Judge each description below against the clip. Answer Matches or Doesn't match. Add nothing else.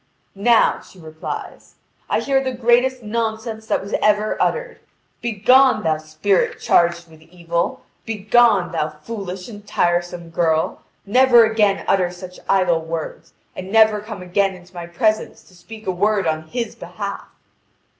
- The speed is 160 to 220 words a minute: Doesn't match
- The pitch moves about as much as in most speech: Matches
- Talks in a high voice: Matches